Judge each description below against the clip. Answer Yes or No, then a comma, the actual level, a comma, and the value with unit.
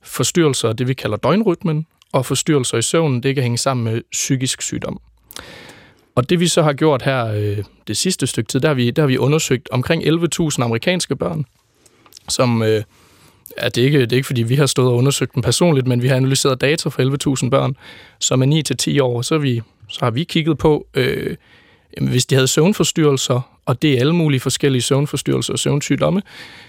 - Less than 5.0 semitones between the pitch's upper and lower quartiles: Yes, average, 3.8 semitones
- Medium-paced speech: Yes, average, 200 wpm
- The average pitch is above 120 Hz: Yes, low, 135 Hz